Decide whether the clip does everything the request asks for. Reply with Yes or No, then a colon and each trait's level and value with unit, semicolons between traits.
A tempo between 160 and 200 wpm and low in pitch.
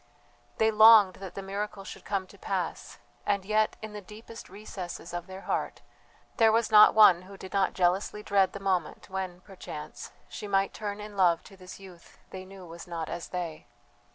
No: average, 190 wpm; high, 195 Hz